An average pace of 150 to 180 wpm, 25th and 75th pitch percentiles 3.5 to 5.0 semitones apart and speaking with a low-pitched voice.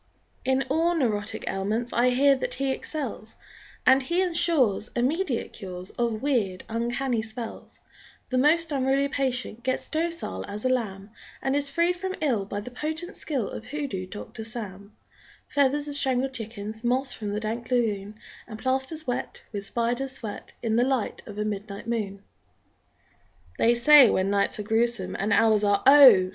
No: average, 165 wpm; average, 4.4 semitones; high, 240 Hz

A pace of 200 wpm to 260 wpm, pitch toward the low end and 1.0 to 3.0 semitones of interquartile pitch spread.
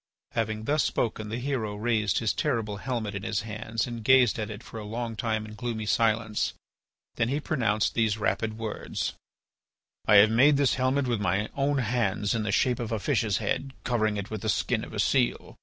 Yes: fast, 205 wpm; low, 110 Hz; narrow, 2.5 semitones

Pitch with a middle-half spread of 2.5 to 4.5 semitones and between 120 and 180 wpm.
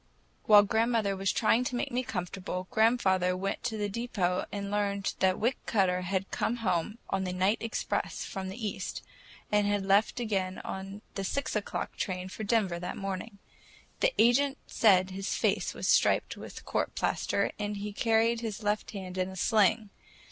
Yes: average, 2.9 semitones; average, 175 wpm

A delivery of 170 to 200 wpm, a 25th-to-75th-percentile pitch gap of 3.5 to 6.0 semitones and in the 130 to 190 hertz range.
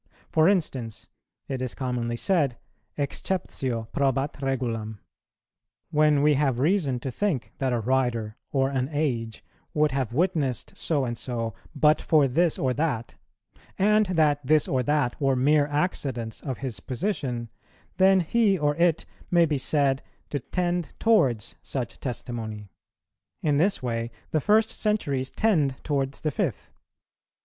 No: average, 140 wpm; average, 4.1 semitones; medium, 140 Hz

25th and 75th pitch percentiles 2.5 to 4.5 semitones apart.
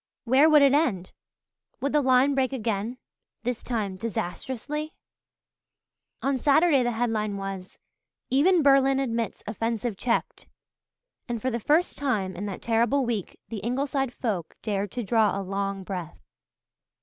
No: average, 4.9 semitones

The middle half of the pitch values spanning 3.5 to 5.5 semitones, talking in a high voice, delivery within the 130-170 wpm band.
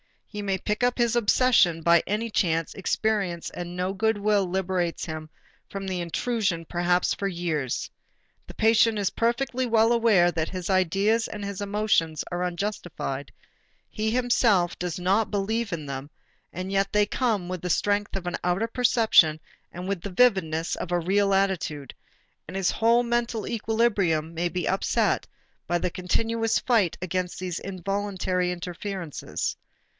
Yes: average, 3.8 semitones; high, 195 Hz; average, 155 wpm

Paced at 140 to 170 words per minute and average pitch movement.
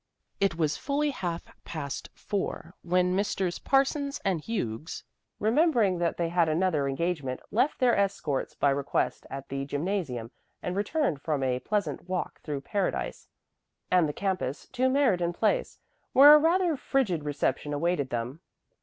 No: average, 145 wpm; wide, 7.2 semitones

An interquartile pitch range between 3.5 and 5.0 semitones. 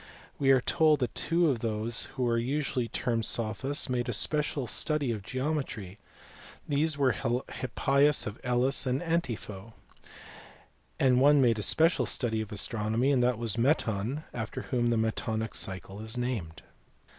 Yes: average, 3.9 semitones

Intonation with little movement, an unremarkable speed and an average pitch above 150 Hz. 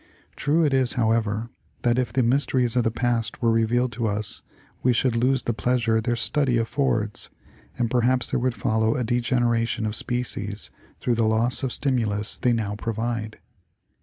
No: narrow, 2.0 semitones; average, 170 wpm; low, 120 Hz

